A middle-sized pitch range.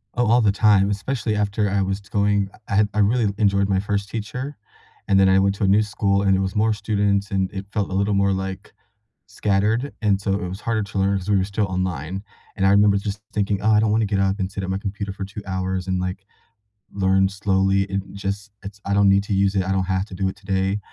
No: narrow, 1.3 semitones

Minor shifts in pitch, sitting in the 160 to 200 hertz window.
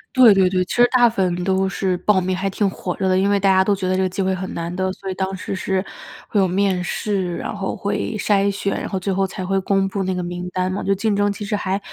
Yes: narrow, 1.2 semitones; high, 190 Hz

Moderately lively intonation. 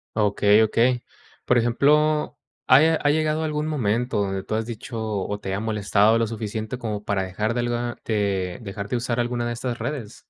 Yes: average, 3.2 semitones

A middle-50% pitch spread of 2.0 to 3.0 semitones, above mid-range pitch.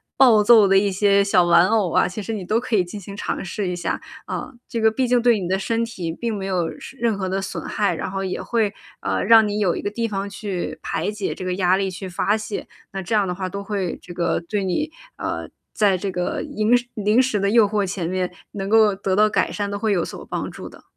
Yes: narrow, 2.6 semitones; high, 200 Hz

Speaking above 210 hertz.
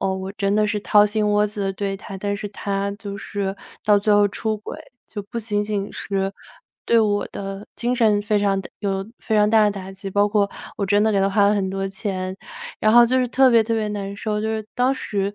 No: high, 205 Hz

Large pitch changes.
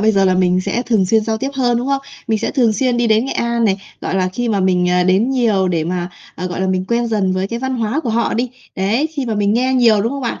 No: average, 4.3 semitones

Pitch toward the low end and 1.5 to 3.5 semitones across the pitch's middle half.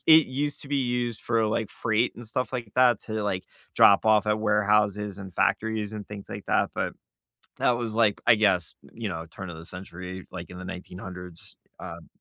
No: low, 105 Hz; average, 3.9 semitones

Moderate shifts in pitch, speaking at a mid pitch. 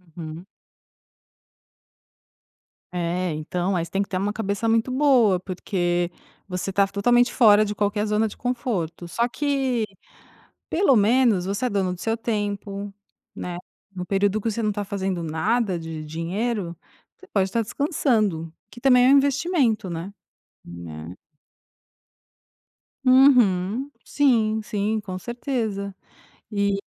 No: average, 4.6 semitones; high, 205 Hz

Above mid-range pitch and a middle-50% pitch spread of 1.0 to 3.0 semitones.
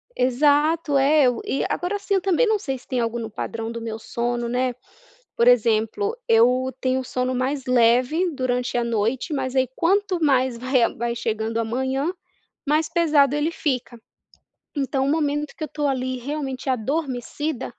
No: very high, 260 Hz; average, 3.7 semitones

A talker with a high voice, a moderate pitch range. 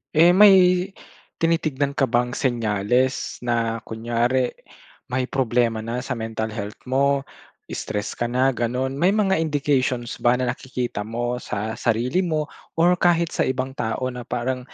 No: low, 125 Hz; average, 3.3 semitones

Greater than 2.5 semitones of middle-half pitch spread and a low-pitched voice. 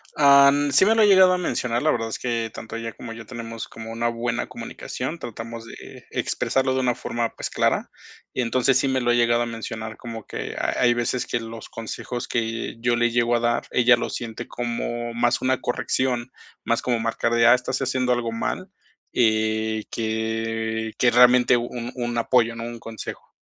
No: narrow, 1.7 semitones; low, 120 Hz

